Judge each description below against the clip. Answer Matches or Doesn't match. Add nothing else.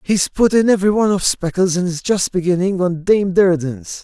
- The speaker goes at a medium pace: Doesn't match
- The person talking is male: Matches